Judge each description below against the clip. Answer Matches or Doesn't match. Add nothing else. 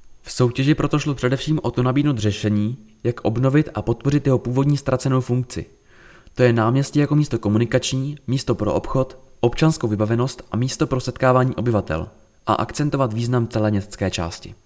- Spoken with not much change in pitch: Doesn't match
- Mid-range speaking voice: Doesn't match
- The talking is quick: Doesn't match